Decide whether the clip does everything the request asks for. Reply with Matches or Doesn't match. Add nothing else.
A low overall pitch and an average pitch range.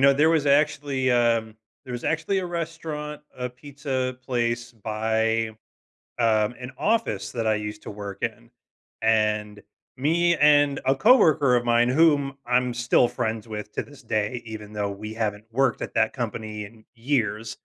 Matches